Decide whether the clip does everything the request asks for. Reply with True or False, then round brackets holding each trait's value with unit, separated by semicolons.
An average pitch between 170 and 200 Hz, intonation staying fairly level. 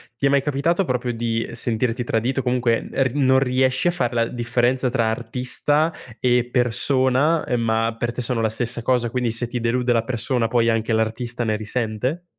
False (120 Hz; 2.0 semitones)